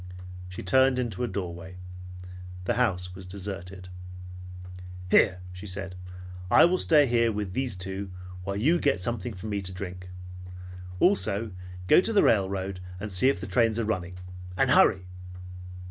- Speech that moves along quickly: No, average, 155 wpm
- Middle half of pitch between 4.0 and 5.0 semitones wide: Yes, average, 4.4 semitones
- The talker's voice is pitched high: No, low, 100 Hz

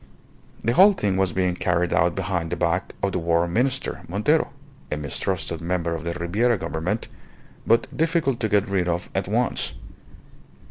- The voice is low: Yes, very low, 90 Hz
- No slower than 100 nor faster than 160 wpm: No, average, 170 wpm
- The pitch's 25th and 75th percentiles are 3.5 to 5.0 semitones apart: Yes, average, 4.6 semitones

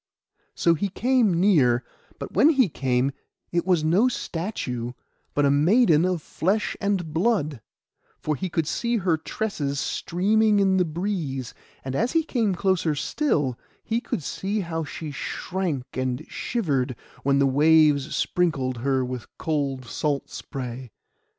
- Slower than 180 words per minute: Yes, average, 145 wpm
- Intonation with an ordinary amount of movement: No, wide, 6.0 semitones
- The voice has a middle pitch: Yes, medium, 160 Hz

